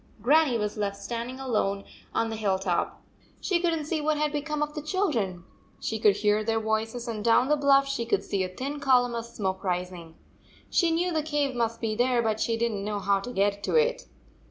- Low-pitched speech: No, high, 235 Hz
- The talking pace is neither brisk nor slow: No, fast, 235 wpm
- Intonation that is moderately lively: No, wide, 6.0 semitones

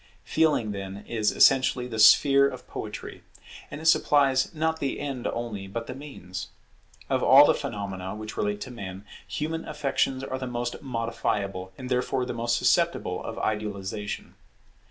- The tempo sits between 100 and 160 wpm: Yes, average, 155 wpm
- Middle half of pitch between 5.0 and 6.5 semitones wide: No, average, 4.6 semitones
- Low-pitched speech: Yes, low, 120 Hz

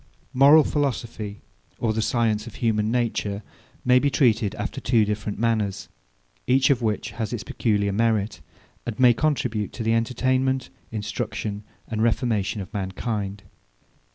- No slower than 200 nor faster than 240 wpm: No, average, 140 wpm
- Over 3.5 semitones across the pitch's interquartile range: No, average, 2.8 semitones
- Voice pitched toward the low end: Yes, low, 115 Hz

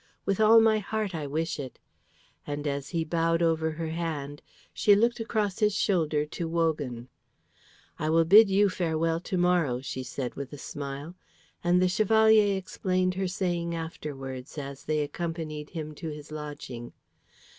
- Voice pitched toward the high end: No, medium, 165 Hz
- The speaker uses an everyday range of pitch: Yes, average, 3.9 semitones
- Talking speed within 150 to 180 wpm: Yes, average, 160 wpm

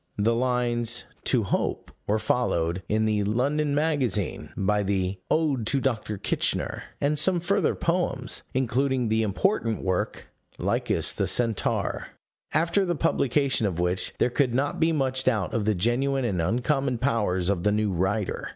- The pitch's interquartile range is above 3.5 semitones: Yes, average, 5.1 semitones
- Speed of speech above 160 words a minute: No, average, 155 wpm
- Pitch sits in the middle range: No, low, 120 Hz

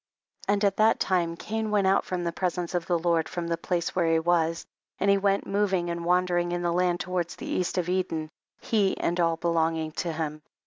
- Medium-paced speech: No, fast, 225 wpm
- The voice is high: No, medium, 175 Hz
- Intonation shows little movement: Yes, narrow, 2.0 semitones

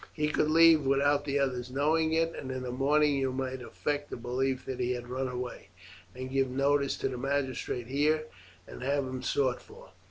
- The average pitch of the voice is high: No, low, 135 Hz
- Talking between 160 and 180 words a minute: No, average, 200 wpm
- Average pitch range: No, narrow, 2.1 semitones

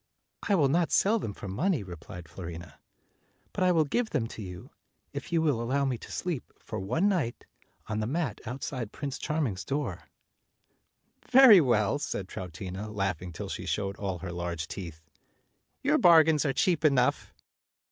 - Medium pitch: No, low, 120 Hz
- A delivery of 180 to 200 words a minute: No, average, 170 wpm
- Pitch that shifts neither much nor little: No, wide, 8.9 semitones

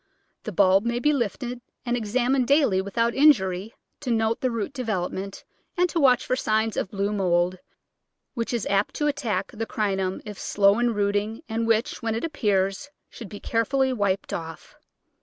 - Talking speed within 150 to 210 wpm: Yes, average, 175 wpm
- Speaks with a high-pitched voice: Yes, high, 225 Hz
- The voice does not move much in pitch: No, average, 3.9 semitones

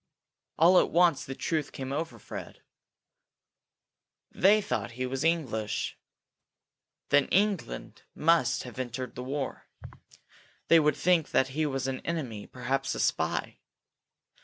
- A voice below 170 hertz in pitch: Yes, low, 135 Hz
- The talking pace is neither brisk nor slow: No, slow, 130 wpm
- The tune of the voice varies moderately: Yes, average, 4.4 semitones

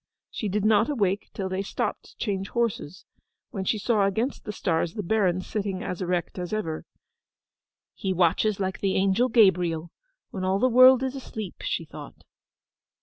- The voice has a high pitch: Yes, high, 195 Hz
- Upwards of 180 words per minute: No, average, 170 wpm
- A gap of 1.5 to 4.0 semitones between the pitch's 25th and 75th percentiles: Yes, average, 2.9 semitones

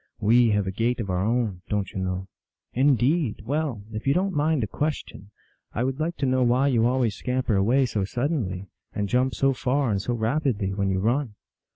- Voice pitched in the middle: No, low, 120 Hz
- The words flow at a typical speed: No, fast, 225 wpm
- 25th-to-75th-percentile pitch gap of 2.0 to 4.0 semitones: No, average, 4.8 semitones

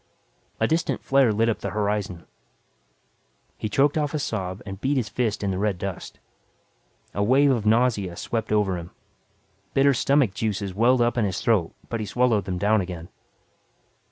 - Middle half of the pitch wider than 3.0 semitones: Yes, average, 4.3 semitones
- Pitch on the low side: Yes, low, 105 Hz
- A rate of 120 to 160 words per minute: No, average, 175 wpm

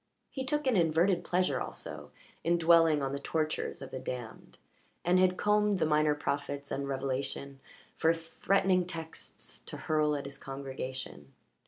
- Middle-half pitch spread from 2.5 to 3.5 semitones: No, average, 4.3 semitones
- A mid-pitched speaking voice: Yes, medium, 155 Hz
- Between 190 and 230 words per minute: No, average, 155 wpm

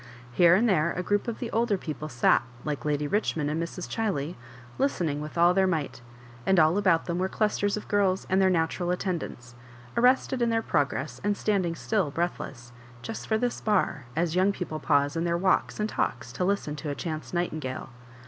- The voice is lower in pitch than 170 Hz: No, medium, 175 Hz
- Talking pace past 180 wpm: Yes, average, 200 wpm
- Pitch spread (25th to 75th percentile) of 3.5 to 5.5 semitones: Yes, average, 4.9 semitones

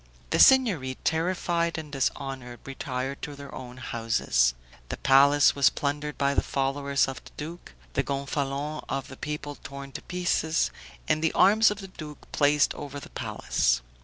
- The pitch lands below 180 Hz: Yes, medium, 140 Hz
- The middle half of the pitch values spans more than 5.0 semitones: No, narrow, 2.5 semitones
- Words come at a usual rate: Yes, average, 160 wpm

